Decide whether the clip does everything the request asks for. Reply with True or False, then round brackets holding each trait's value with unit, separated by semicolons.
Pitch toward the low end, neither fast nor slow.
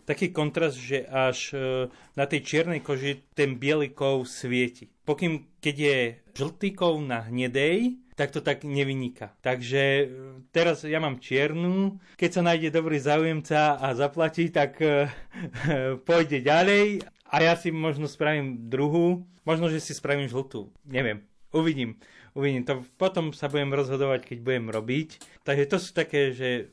False (145 Hz; 145 wpm)